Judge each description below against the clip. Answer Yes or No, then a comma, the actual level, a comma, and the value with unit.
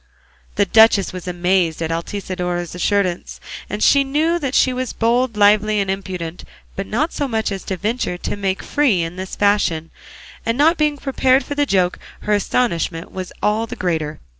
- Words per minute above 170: Yes, average, 185 wpm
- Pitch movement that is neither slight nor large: No, wide, 5.8 semitones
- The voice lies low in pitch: No, high, 200 Hz